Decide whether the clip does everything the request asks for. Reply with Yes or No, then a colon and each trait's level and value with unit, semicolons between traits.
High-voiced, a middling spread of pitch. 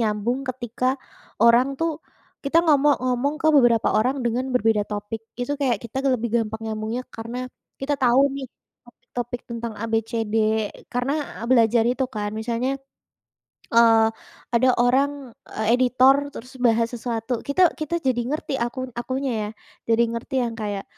No: high, 240 Hz; narrow, 2.3 semitones